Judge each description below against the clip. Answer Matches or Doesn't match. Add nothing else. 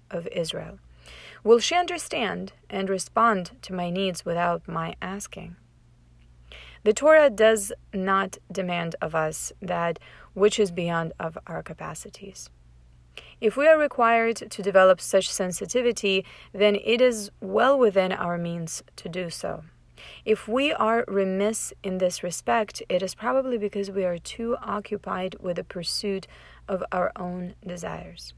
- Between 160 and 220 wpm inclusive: Doesn't match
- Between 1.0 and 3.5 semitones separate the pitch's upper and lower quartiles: Doesn't match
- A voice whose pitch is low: Doesn't match